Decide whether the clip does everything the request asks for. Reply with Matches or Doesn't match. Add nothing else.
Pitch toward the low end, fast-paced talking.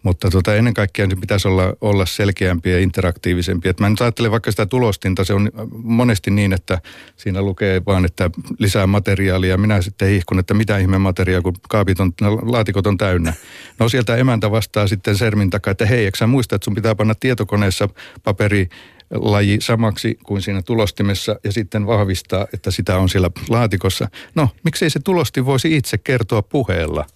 Matches